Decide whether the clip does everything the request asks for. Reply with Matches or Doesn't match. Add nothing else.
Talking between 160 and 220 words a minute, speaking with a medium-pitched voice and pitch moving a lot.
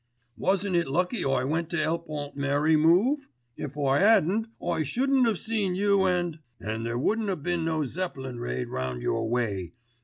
Matches